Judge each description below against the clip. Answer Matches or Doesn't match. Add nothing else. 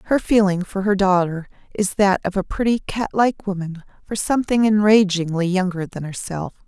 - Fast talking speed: Doesn't match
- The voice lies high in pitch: Matches